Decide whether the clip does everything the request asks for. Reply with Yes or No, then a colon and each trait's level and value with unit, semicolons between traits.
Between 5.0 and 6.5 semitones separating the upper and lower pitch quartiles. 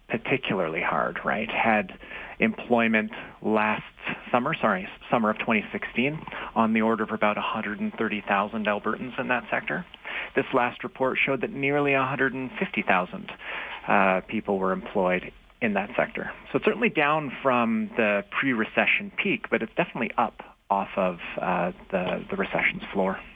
No: average, 3.8 semitones